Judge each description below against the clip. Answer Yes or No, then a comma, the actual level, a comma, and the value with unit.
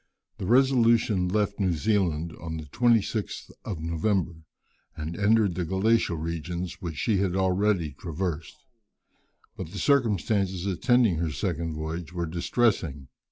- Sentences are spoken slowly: Yes, slow, 130 wpm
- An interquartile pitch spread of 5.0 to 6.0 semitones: No, average, 4.2 semitones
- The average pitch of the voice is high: No, very low, 90 Hz